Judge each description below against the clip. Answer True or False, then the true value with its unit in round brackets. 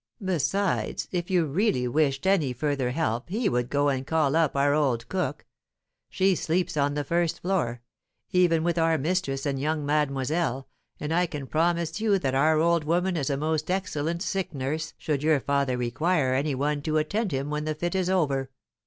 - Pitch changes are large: False (3.9 semitones)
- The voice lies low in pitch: False (155 Hz)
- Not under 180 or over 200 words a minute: True (190 wpm)